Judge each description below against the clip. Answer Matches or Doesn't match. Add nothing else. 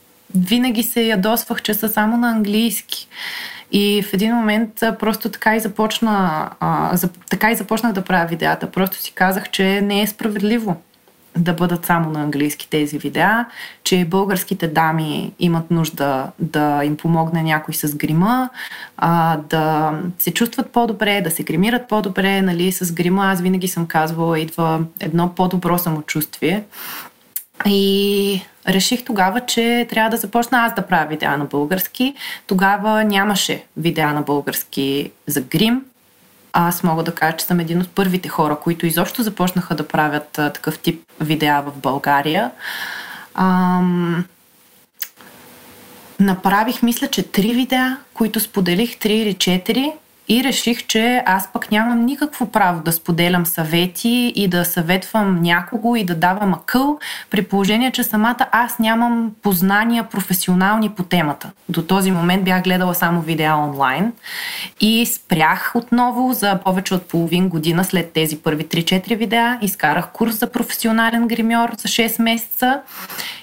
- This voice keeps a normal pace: Matches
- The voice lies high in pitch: Matches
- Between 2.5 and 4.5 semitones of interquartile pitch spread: Doesn't match